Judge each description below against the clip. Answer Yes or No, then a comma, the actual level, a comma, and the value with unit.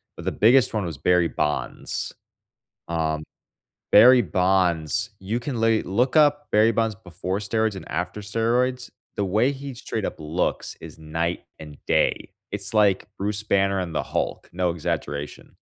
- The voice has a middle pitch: No, low, 100 Hz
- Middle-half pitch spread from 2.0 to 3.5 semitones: No, average, 4.9 semitones